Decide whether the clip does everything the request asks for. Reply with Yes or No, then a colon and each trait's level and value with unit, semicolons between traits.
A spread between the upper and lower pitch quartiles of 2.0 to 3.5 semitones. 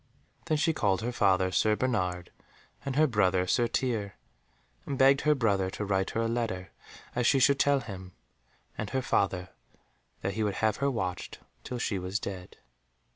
No: average, 5.2 semitones